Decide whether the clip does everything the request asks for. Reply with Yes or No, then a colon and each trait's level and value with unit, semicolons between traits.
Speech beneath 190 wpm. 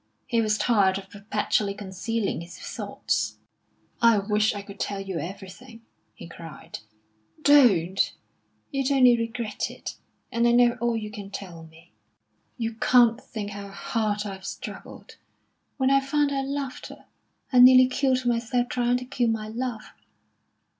Yes: average, 150 wpm